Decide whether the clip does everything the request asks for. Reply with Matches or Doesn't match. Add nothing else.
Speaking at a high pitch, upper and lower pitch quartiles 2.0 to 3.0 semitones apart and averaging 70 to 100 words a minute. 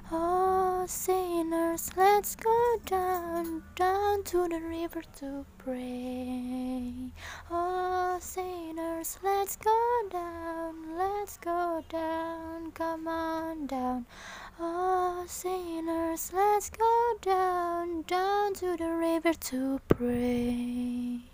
Matches